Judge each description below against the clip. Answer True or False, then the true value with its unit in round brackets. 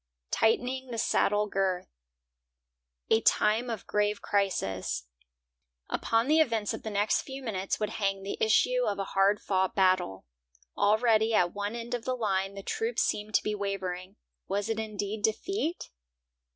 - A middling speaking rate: True (155 wpm)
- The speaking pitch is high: True (210 Hz)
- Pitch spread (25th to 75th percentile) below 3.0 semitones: True (2.6 semitones)